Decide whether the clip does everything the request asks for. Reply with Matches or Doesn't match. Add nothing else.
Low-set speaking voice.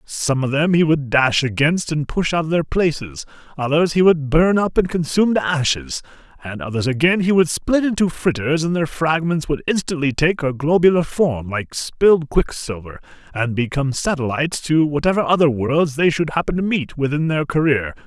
Doesn't match